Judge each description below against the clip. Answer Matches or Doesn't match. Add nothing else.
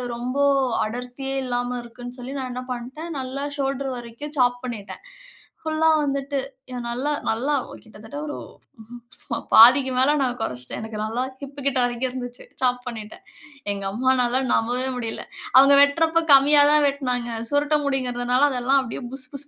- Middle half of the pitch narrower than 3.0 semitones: Matches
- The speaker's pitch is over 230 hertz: Matches